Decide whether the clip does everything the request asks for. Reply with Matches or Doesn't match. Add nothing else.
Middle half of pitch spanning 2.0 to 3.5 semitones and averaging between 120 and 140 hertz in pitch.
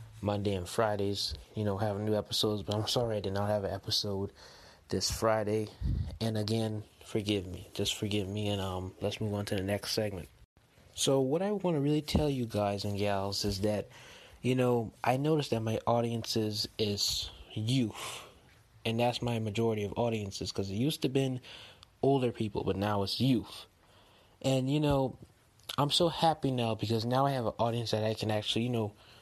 Doesn't match